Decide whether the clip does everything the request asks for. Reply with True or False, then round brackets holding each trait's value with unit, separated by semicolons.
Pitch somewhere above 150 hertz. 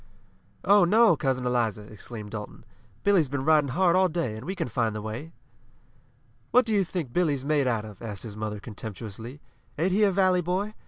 False (140 Hz)